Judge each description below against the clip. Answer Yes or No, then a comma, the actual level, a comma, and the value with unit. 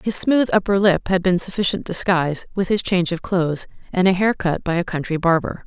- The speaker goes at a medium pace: No, fast, 220 wpm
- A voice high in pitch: No, medium, 180 Hz